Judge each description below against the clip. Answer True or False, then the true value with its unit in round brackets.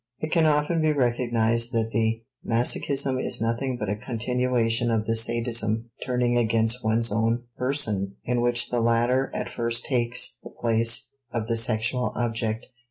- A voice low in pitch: True (115 Hz)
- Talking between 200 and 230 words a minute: False (160 wpm)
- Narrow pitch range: True (1.7 semitones)